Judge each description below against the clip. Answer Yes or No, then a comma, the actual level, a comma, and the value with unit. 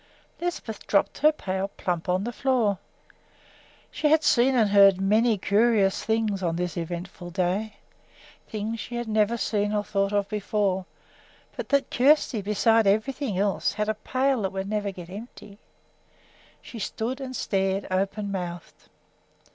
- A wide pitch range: No, average, 3.0 semitones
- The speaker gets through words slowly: No, average, 150 wpm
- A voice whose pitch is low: No, high, 210 Hz